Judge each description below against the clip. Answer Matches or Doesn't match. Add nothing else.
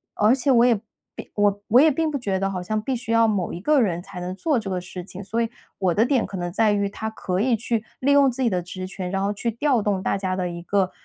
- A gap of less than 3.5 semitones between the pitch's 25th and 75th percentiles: Doesn't match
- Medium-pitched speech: Doesn't match